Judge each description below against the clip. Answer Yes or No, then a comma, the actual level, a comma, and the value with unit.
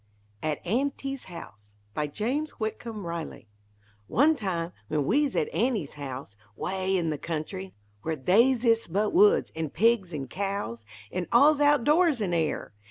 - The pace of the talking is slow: No, average, 155 wpm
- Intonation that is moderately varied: No, wide, 8.4 semitones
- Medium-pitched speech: No, high, 195 Hz